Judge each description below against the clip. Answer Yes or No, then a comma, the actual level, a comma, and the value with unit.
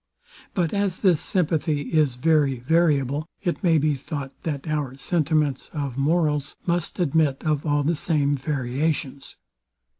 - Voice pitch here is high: No, medium, 150 Hz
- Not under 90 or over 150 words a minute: Yes, average, 140 wpm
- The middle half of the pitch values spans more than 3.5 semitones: No, average, 2.7 semitones